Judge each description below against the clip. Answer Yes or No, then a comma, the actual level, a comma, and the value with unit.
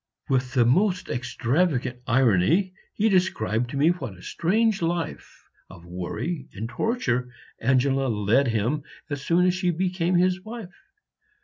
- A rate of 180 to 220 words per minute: No, average, 140 wpm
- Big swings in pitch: Yes, wide, 6.8 semitones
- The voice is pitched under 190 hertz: Yes, medium, 140 Hz